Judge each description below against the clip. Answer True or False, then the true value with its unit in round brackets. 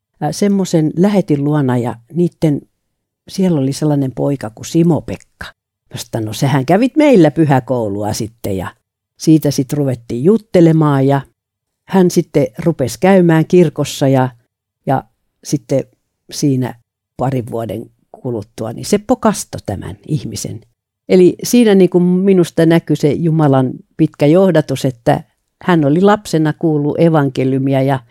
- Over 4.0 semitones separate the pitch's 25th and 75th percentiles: True (5.2 semitones)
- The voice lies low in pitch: False (145 Hz)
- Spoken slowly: False (125 wpm)